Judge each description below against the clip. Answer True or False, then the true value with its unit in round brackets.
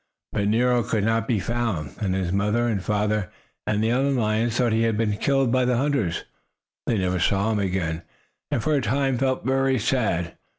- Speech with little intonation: False (3.6 semitones)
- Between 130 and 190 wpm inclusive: False (200 wpm)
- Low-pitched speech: True (110 Hz)